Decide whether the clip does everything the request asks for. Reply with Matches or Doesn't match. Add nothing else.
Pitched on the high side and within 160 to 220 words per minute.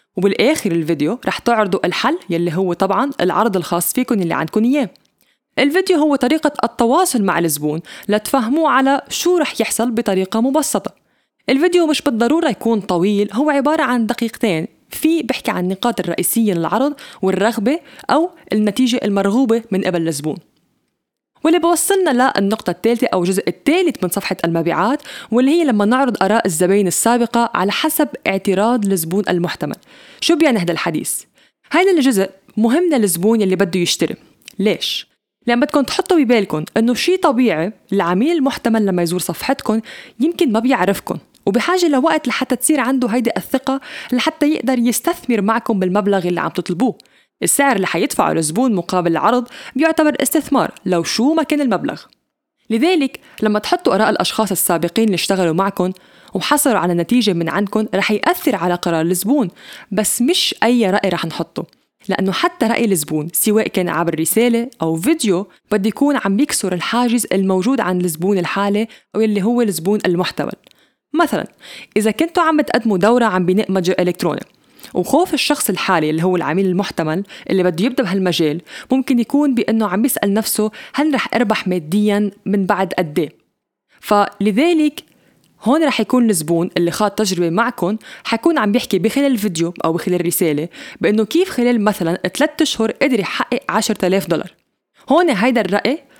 Doesn't match